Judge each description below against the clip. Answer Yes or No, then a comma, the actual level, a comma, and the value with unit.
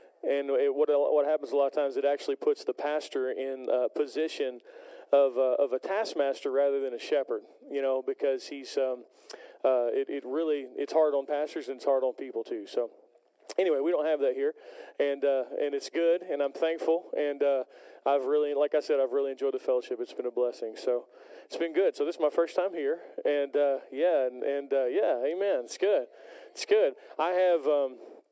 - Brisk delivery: Yes, fast, 220 wpm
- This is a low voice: No, medium, 160 Hz